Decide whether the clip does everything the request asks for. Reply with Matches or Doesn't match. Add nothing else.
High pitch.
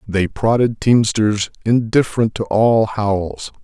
Doesn't match